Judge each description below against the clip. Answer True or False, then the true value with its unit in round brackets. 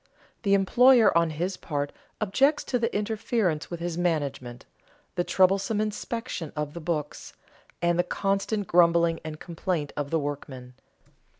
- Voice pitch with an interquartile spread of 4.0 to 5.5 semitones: True (4.7 semitones)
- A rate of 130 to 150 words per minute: True (140 wpm)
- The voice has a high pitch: False (175 Hz)